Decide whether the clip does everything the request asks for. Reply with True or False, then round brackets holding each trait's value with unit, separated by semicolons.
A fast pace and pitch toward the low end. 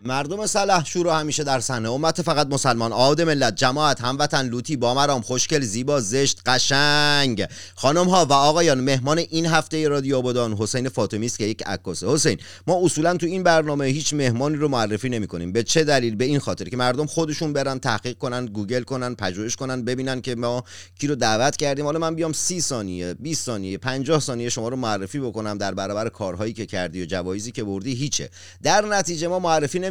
True (200 wpm; 130 Hz)